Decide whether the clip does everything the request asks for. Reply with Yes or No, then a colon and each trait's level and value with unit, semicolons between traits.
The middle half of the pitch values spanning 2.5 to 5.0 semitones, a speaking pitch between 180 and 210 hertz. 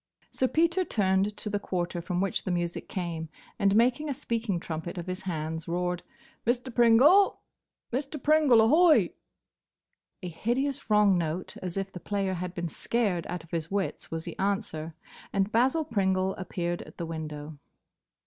No: wide, 5.4 semitones; high, 190 Hz